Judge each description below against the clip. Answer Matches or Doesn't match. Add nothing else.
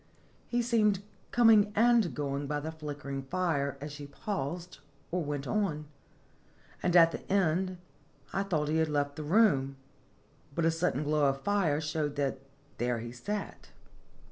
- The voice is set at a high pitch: Doesn't match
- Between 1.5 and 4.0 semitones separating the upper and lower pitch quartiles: Doesn't match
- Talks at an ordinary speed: Matches